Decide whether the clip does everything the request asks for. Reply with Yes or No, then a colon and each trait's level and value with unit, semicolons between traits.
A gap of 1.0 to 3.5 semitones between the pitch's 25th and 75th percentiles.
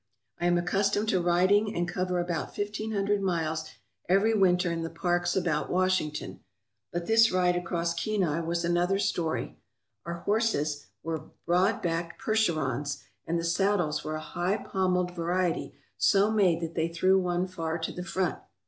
Yes: narrow, 2.5 semitones